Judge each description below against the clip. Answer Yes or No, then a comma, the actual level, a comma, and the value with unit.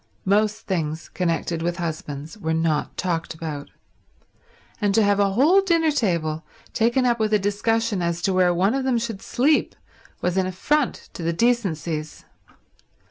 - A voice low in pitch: No, high, 190 Hz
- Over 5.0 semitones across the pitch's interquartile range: Yes, wide, 5.5 semitones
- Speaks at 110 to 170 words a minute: Yes, average, 160 wpm